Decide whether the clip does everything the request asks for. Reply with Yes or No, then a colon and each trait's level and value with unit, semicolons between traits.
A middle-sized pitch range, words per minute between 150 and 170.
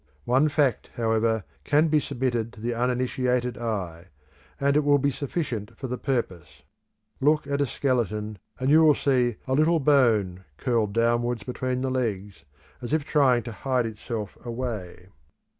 Yes: average, 3.6 semitones; average, 160 wpm